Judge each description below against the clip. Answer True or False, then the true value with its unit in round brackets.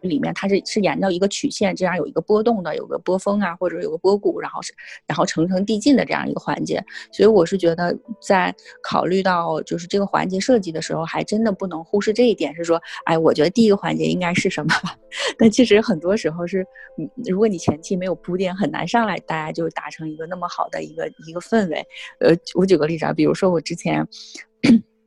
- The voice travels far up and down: False (4.8 semitones)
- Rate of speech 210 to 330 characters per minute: False (345 characters per minute)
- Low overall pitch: False (190 Hz)